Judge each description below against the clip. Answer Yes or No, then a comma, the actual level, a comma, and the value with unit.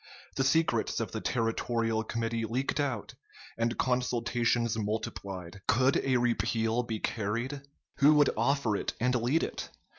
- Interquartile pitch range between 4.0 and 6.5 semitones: No, narrow, 2.5 semitones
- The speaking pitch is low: Yes, low, 120 Hz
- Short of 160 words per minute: Yes, average, 140 wpm